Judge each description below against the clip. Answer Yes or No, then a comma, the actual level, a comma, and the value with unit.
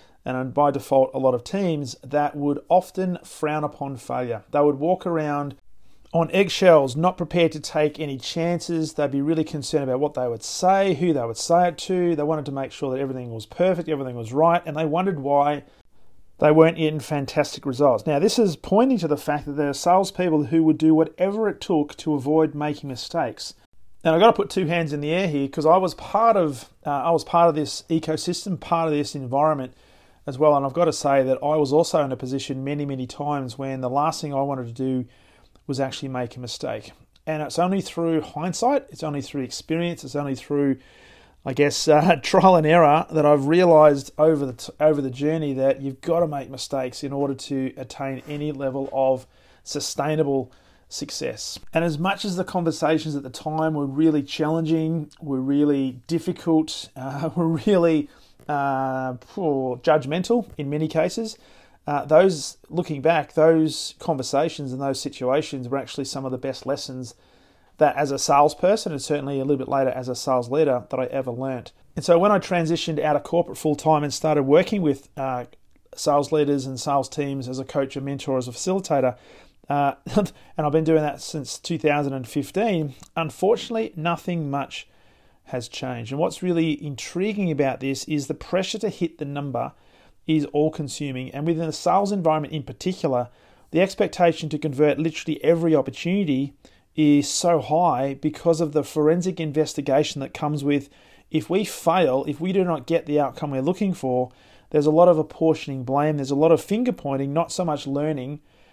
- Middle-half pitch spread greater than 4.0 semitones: No, average, 3.2 semitones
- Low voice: No, medium, 150 Hz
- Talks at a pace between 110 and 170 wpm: No, average, 195 wpm